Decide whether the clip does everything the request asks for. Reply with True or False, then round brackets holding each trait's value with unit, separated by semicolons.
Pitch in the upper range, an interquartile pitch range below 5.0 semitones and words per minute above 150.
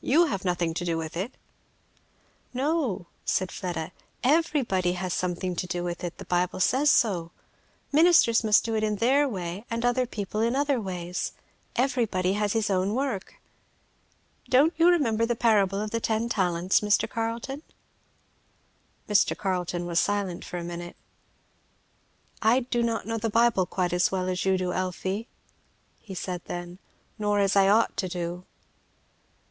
True (200 Hz; 4.5 semitones; 160 wpm)